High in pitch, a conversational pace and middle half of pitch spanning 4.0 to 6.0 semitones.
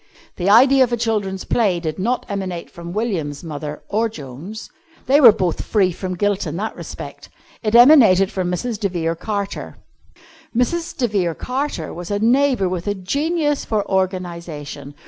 Yes: high, 200 Hz; average, 165 wpm; average, 5.1 semitones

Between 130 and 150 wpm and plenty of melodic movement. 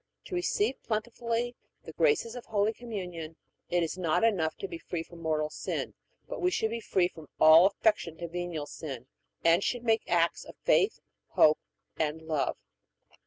No: average, 170 wpm; wide, 6.3 semitones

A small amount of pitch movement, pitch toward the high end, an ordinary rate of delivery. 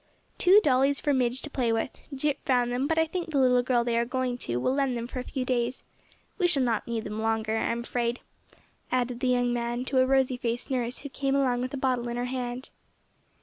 No: narrow, 1.9 semitones; very high, 250 Hz; fast, 235 wpm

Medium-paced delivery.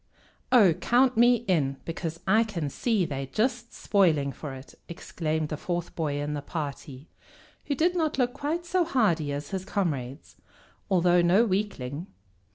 Yes: average, 160 wpm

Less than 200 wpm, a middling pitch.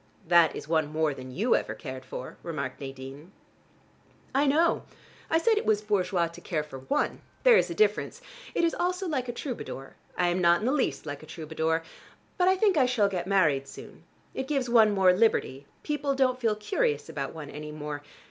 No: fast, 205 wpm; medium, 180 Hz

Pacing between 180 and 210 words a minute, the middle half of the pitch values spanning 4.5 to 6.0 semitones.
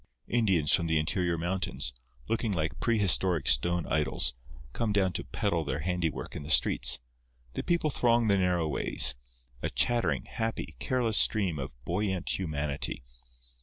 No: average, 145 wpm; average, 5.2 semitones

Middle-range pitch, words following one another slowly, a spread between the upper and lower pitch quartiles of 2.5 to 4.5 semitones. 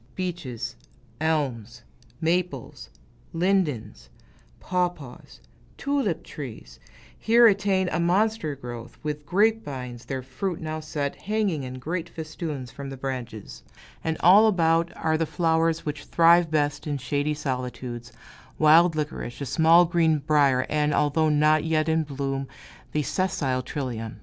Yes: medium, 155 Hz; slow, 130 wpm; average, 4.1 semitones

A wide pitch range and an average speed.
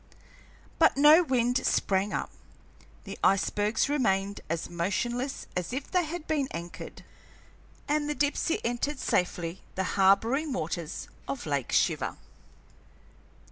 No: wide, 7.4 semitones; slow, 120 wpm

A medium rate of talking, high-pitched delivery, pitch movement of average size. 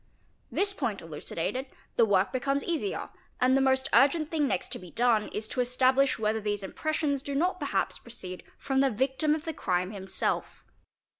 Yes: average, 175 wpm; very high, 260 Hz; average, 5.0 semitones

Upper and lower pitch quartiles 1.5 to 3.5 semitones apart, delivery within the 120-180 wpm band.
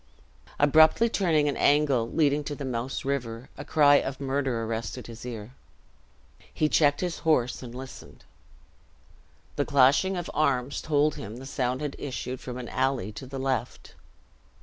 Yes: average, 2.9 semitones; average, 155 wpm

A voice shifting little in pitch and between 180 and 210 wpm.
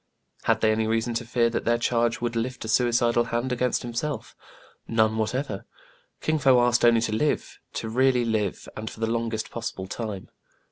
Yes: narrow, 1.6 semitones; average, 190 wpm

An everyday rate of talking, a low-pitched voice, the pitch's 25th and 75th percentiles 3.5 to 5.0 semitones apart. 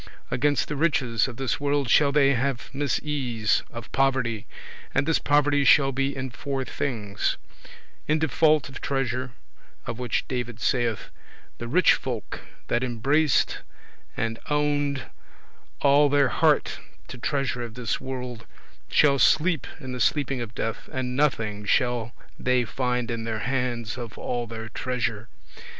No: average, 155 wpm; low, 130 Hz; average, 3.1 semitones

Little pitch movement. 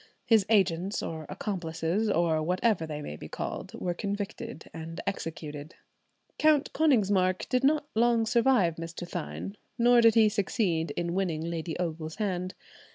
No: average, 5.3 semitones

